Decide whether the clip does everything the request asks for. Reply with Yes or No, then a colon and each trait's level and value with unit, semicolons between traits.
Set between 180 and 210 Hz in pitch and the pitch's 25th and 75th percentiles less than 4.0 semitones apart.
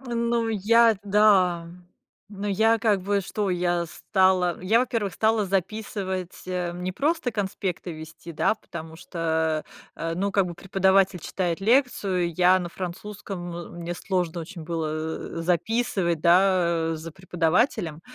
Yes: medium, 185 Hz; average, 3.2 semitones